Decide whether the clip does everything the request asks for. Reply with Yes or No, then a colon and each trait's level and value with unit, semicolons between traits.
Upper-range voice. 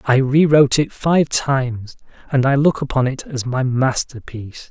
No: low, 135 Hz